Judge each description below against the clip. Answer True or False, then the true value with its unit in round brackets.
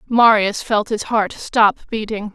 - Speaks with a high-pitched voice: True (215 Hz)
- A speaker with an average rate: True (155 wpm)